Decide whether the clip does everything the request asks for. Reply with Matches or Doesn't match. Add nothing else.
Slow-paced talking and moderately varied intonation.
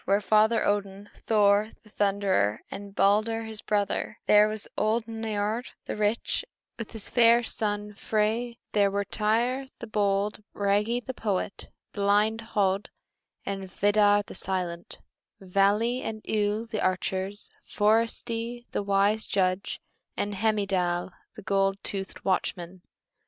Doesn't match